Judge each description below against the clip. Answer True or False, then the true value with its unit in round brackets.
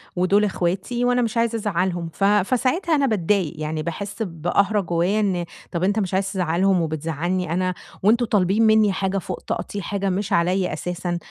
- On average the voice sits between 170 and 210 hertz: True (190 Hz)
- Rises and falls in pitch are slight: False (3.1 semitones)